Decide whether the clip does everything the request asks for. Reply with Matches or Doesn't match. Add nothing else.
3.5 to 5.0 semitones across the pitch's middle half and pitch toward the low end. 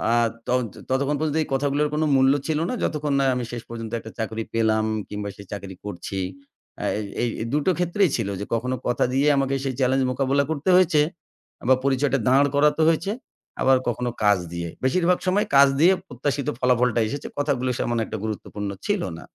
Matches